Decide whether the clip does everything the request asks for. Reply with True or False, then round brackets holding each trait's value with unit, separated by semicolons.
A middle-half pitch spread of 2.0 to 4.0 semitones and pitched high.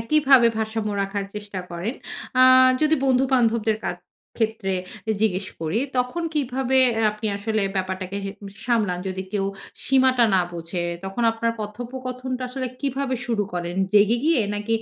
False (4.5 semitones; 225 Hz)